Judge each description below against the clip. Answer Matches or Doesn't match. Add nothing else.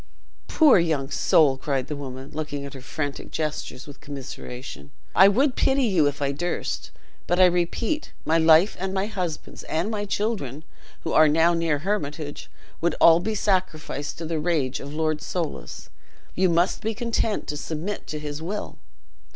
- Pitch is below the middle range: Doesn't match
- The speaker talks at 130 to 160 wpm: Doesn't match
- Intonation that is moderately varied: Matches